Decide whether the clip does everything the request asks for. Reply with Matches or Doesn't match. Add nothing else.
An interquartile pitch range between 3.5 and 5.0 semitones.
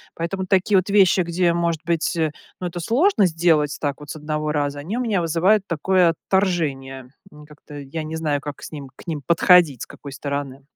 Matches